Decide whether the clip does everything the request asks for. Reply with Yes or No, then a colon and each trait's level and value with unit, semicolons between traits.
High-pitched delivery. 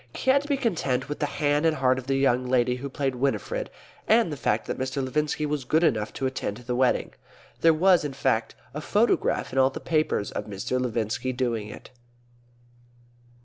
No: low, 135 Hz